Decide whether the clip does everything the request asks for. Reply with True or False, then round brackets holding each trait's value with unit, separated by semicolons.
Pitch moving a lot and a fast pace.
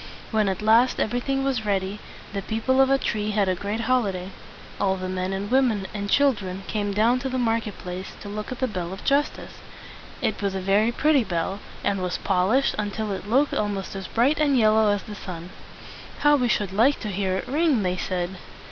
False (4.4 semitones; 210 wpm)